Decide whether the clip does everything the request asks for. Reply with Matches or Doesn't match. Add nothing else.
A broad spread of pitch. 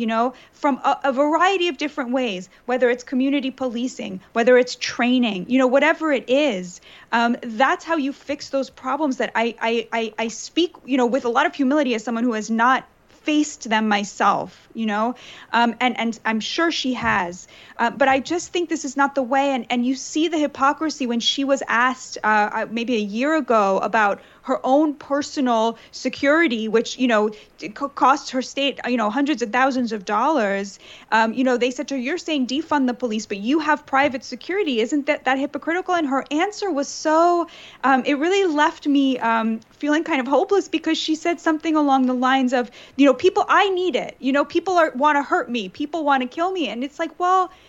Doesn't match